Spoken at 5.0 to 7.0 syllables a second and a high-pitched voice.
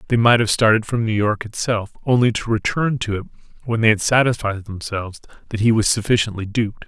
No: 6.0 syllables/s; low, 110 Hz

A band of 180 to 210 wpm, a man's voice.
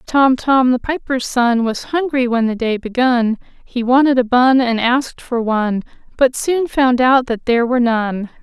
No: average, 190 wpm; female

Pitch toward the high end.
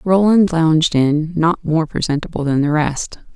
No: medium, 160 Hz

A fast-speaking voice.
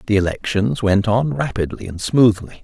No: average, 160 wpm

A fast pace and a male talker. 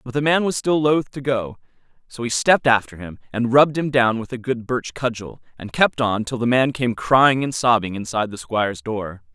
Yes: fast, 230 wpm; male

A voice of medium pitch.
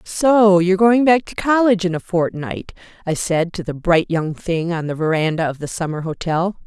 Yes: medium, 180 Hz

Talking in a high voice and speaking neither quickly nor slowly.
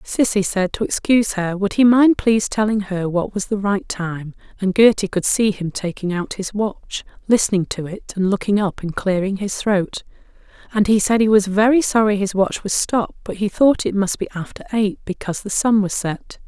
No: high, 200 Hz; fast, 215 wpm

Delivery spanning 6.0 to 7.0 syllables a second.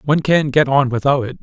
Yes: 6.2 syllables/s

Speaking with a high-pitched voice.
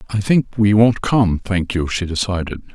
No: low, 100 Hz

